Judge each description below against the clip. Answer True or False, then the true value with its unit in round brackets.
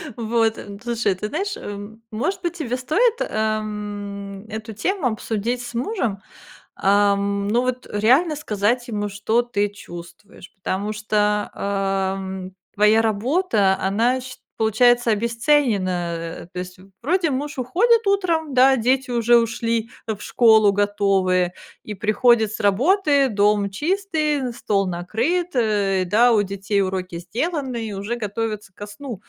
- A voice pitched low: False (220 Hz)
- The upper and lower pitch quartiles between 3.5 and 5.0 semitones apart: True (3.9 semitones)